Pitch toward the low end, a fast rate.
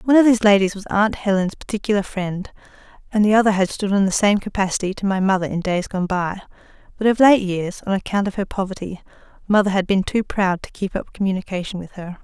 No: high, 195 Hz; fast, 220 wpm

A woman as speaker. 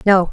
Yes: female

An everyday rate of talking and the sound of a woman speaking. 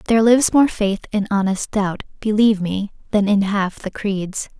Yes: average, 185 wpm; female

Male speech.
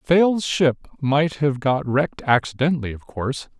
Yes: male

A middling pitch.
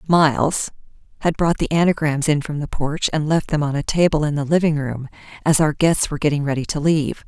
Yes: medium, 150 Hz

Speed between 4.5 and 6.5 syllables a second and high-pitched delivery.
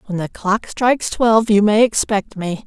Yes: 4.8 syllables/s; high, 210 Hz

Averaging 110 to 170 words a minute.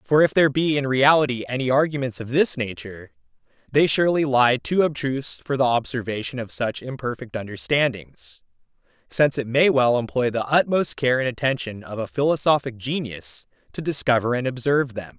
Yes: average, 165 wpm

